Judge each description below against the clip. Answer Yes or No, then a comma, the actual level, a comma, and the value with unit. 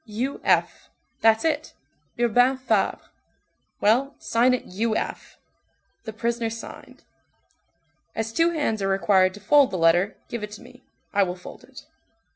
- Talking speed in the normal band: Yes, average, 150 wpm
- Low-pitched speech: No, high, 225 Hz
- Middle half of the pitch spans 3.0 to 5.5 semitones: Yes, average, 3.6 semitones